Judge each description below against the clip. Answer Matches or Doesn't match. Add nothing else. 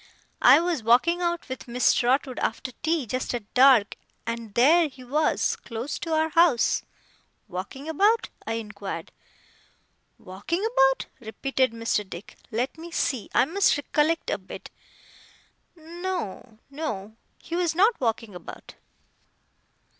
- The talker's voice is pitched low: Doesn't match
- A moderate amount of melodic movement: Doesn't match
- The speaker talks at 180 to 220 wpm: Doesn't match